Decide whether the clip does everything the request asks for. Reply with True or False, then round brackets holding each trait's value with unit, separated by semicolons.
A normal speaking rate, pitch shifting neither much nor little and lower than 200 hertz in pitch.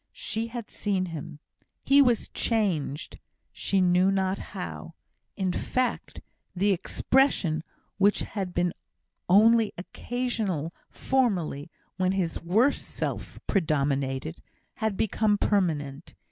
False (105 wpm; 4.9 semitones; 190 Hz)